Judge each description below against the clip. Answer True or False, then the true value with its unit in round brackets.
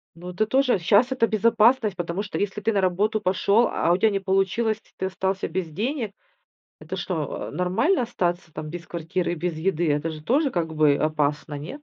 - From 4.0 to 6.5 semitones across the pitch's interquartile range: True (4.5 semitones)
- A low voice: False (190 Hz)